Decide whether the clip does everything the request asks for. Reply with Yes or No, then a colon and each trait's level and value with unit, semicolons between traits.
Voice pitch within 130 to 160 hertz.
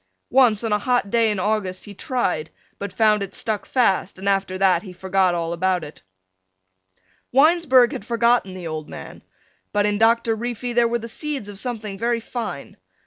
No: high, 210 Hz